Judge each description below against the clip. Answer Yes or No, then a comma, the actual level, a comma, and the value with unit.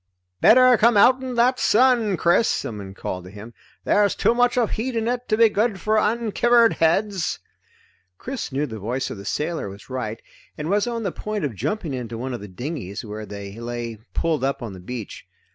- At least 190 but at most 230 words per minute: Yes, average, 200 wpm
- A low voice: No, medium, 165 Hz